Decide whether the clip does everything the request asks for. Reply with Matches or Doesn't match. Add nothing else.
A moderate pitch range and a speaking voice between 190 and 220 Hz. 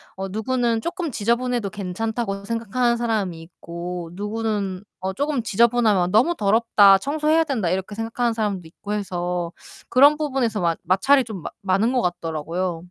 Matches